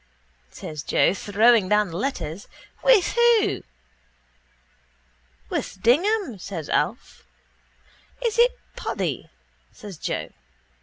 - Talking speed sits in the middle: No, slow, 95 wpm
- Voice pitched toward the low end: No, high, 225 Hz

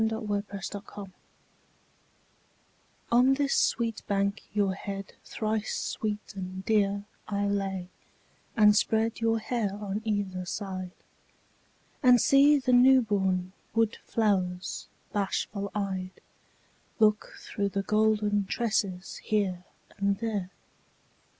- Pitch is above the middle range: Yes, high, 205 Hz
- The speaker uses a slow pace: Yes, slow, 105 wpm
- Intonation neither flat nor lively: No, narrow, 2.1 semitones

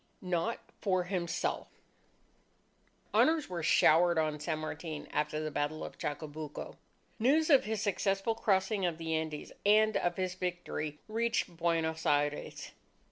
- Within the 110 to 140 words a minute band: Yes, slow, 135 wpm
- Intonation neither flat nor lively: Yes, average, 4.6 semitones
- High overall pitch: No, medium, 170 Hz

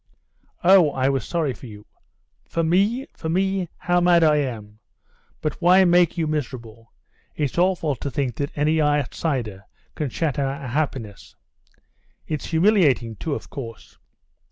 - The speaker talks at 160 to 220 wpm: No, average, 145 wpm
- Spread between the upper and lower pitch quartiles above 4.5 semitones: Yes, average, 5.0 semitones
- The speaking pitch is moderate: Yes, medium, 150 Hz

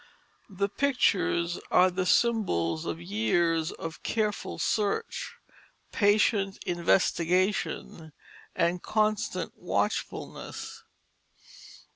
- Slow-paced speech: Yes, slow, 75 wpm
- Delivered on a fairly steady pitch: No, average, 4.2 semitones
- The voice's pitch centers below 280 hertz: Yes, medium, 185 Hz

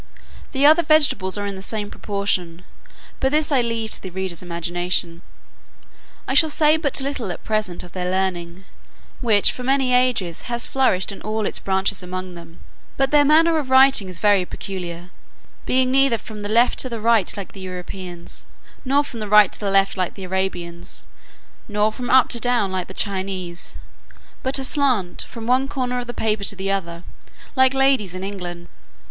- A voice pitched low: No, high, 205 Hz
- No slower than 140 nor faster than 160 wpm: No, average, 185 wpm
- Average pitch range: No, wide, 5.7 semitones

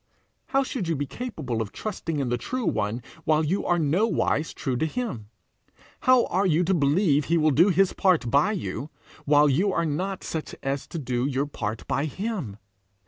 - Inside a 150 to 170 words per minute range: No, average, 195 wpm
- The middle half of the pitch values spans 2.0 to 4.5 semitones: No, wide, 5.6 semitones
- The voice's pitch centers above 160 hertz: No, medium, 155 Hz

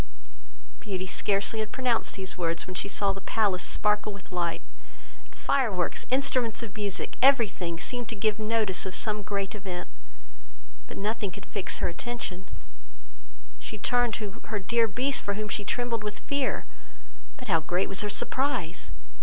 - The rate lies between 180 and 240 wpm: No, average, 165 wpm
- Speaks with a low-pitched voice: No, high, 210 Hz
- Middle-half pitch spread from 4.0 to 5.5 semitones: No, average, 3.4 semitones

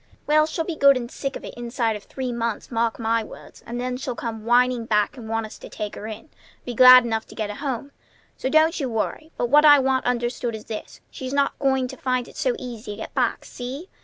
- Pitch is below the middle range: No, high, 245 Hz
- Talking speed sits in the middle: No, fast, 250 wpm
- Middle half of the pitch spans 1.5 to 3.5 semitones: Yes, average, 3.1 semitones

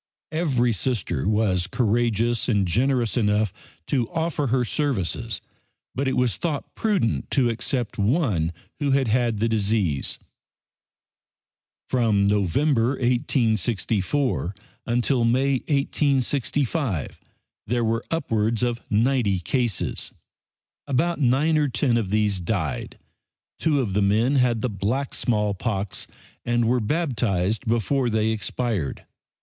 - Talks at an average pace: No, slow, 115 wpm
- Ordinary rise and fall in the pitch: Yes, average, 4.1 semitones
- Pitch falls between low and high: No, low, 120 Hz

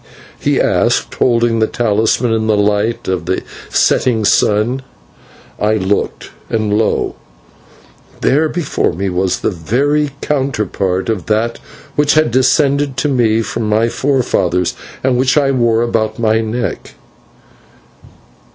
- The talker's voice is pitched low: Yes, low, 115 Hz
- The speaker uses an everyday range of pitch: Yes, average, 3.7 semitones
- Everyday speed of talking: No, slow, 130 wpm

